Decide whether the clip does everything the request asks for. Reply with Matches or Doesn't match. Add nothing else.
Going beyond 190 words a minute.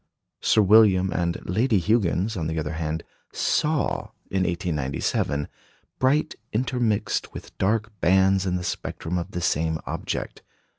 Doesn't match